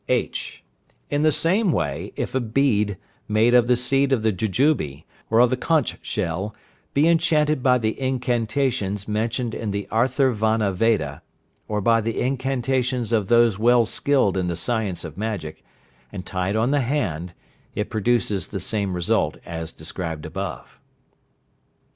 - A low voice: Yes, low, 115 Hz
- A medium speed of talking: Yes, average, 155 wpm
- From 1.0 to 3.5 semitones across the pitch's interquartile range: No, average, 4.8 semitones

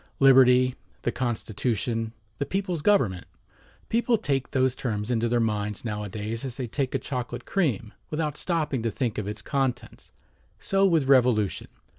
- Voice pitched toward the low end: Yes, low, 125 Hz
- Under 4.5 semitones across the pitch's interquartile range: Yes, average, 3.9 semitones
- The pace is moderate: Yes, average, 150 wpm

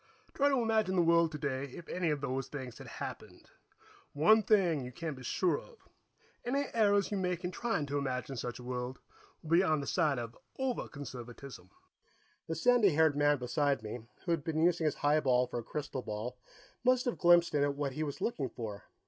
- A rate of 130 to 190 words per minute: No, fast, 205 wpm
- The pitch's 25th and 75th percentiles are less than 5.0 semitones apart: No, wide, 5.6 semitones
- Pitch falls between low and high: Yes, medium, 150 Hz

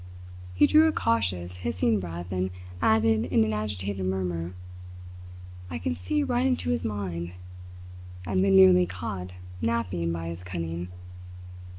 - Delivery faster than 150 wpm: No, average, 145 wpm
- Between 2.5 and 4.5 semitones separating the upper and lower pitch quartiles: Yes, average, 3.7 semitones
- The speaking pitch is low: Yes, very low, 95 Hz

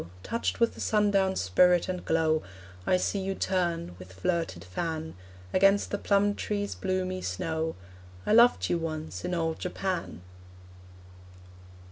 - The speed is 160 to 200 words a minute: No, slow, 135 wpm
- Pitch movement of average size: Yes, average, 3.5 semitones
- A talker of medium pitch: Yes, medium, 180 Hz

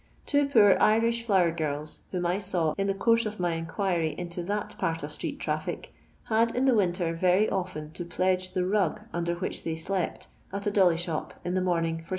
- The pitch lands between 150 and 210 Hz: Yes, medium, 185 Hz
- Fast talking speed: Yes, fast, 210 wpm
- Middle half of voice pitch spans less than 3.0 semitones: No, average, 3.5 semitones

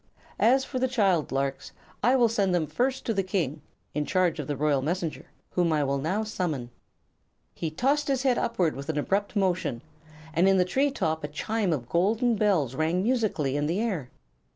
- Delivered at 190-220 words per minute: Yes, average, 200 wpm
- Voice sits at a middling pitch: Yes, medium, 180 Hz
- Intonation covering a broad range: Yes, wide, 6.9 semitones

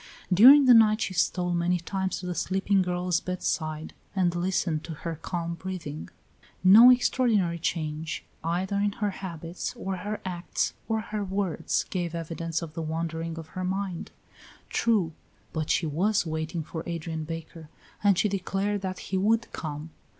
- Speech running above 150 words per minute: Yes, average, 160 wpm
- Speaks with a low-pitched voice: No, medium, 180 Hz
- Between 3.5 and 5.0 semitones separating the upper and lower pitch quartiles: No, average, 3.1 semitones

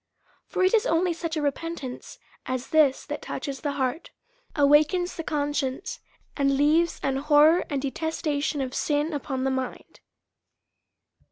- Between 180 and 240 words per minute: No, average, 150 wpm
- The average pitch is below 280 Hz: No, very high, 295 Hz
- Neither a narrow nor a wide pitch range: Yes, average, 3.1 semitones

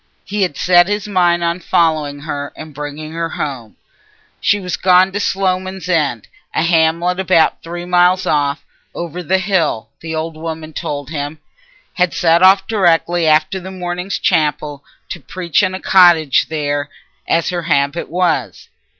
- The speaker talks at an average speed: Yes, average, 150 wpm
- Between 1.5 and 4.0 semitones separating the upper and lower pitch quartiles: Yes, average, 3.1 semitones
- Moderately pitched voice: Yes, medium, 170 Hz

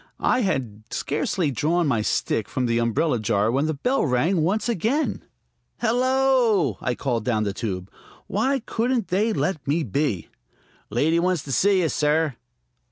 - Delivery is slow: No, average, 160 wpm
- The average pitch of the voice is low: No, medium, 155 Hz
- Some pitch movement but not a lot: No, wide, 9.0 semitones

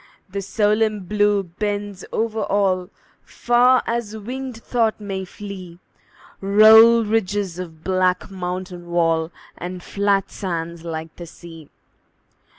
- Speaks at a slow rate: Yes, slow, 115 wpm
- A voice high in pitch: Yes, high, 195 Hz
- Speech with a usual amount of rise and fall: Yes, average, 3.2 semitones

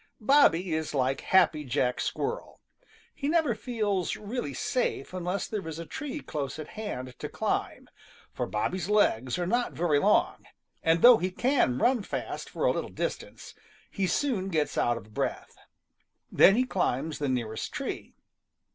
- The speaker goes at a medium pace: Yes, average, 160 wpm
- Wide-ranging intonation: Yes, wide, 8.0 semitones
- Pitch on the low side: No, medium, 180 Hz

